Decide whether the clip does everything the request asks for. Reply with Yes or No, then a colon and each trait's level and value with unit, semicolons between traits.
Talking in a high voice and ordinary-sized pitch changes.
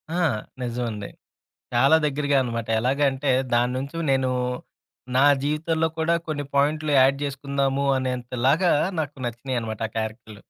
No: low, 135 Hz; average, 3.2 semitones